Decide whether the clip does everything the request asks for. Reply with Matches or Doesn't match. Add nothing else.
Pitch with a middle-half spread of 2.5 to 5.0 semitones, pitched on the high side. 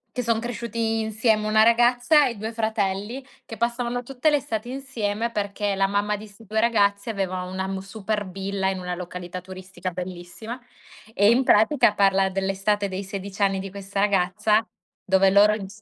Matches